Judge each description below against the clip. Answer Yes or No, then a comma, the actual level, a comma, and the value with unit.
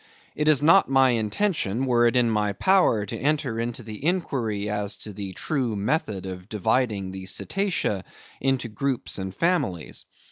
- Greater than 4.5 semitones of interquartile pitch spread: Yes, wide, 5.4 semitones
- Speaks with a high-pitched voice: No, low, 115 Hz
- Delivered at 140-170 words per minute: Yes, average, 165 wpm